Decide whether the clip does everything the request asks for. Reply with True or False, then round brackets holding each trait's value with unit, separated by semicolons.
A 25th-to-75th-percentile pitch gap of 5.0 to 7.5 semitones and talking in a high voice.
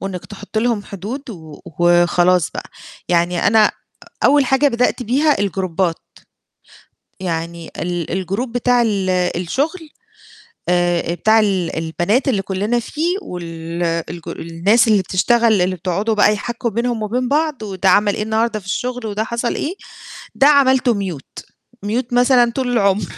True (5.3 semitones; 205 Hz)